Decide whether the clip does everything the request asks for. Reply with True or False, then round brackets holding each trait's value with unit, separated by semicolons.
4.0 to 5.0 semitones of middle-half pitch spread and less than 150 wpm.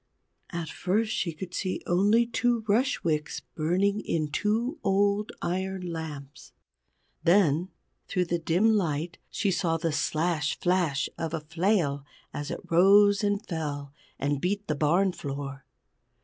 True (4.7 semitones; 140 wpm)